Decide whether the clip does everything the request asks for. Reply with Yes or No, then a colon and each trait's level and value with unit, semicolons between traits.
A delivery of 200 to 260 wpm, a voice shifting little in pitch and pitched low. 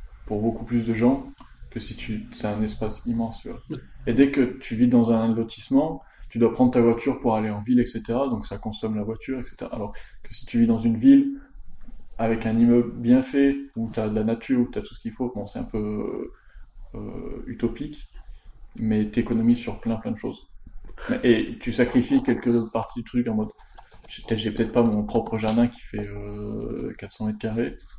Yes: average, 210 wpm; narrow, 1.9 semitones; low, 115 Hz